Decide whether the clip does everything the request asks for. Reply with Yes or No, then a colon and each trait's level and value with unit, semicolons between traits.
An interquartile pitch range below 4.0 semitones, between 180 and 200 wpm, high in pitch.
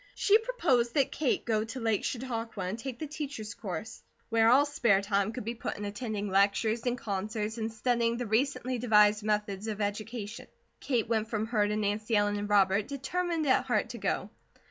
Yes: average, 3.1 semitones; average, 190 wpm; high, 225 Hz